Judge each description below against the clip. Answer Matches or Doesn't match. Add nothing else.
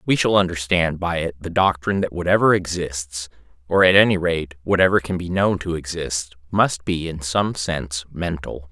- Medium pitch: Doesn't match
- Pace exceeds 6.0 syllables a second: Doesn't match